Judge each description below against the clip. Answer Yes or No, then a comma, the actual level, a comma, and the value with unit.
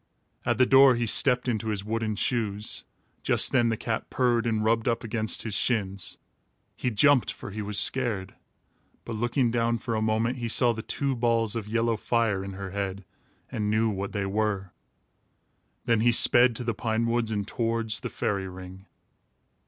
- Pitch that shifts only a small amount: Yes, narrow, 2.3 semitones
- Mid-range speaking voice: No, low, 115 Hz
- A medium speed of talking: Yes, average, 185 wpm